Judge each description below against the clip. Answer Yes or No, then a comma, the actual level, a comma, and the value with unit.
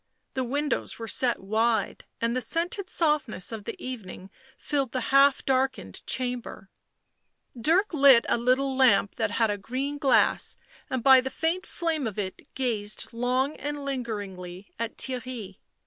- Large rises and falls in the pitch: No, average, 3.7 semitones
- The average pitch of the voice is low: No, very high, 255 Hz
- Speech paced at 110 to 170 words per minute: Yes, average, 150 wpm